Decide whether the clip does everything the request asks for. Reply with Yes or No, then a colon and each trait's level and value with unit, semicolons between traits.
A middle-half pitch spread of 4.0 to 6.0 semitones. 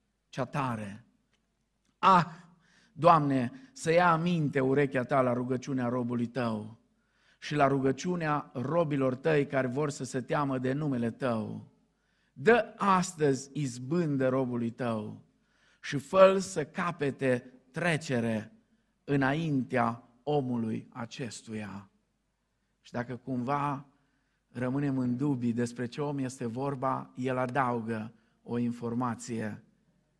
No: average, 3.4 semitones